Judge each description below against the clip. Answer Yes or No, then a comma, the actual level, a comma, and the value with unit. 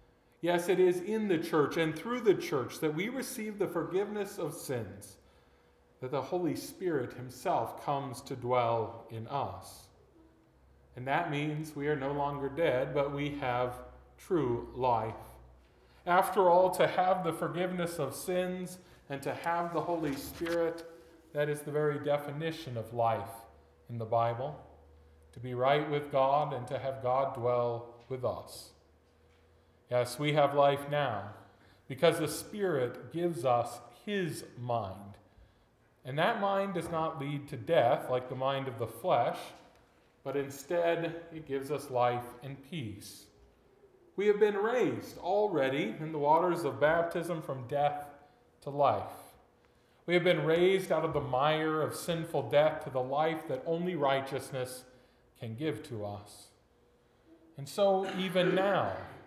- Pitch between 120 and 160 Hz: Yes, medium, 140 Hz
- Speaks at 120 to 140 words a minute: No, average, 150 wpm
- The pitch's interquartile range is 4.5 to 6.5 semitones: Yes, wide, 5.6 semitones